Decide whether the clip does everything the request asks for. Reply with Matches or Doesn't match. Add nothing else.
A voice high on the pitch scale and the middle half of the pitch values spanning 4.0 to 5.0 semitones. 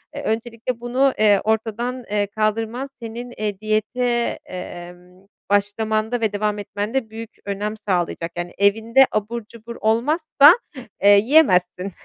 Doesn't match